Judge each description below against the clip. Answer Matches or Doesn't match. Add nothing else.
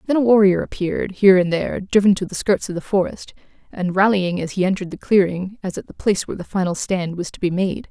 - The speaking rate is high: Matches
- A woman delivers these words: Matches